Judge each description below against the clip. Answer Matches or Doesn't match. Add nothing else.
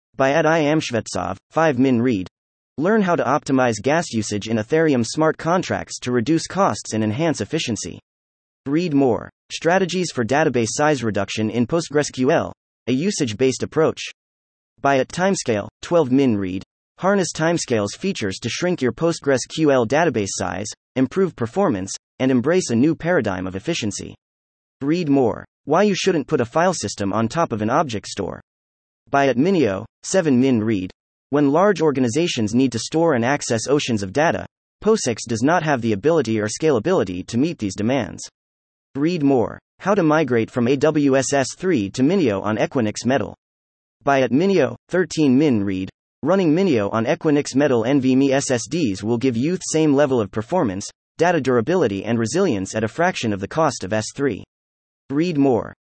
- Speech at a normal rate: Matches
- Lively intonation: Matches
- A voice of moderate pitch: Doesn't match